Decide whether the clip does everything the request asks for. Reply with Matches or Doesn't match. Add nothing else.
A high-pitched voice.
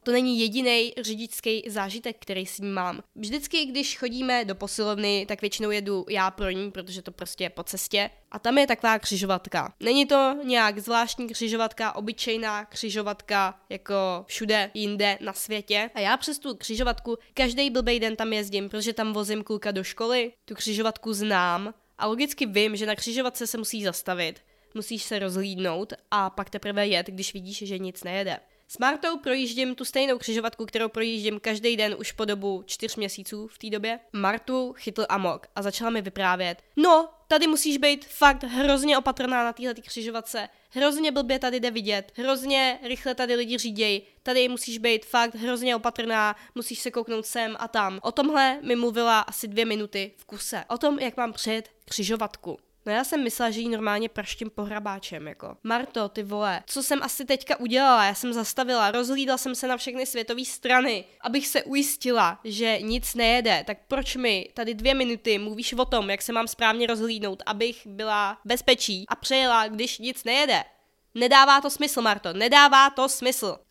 Matches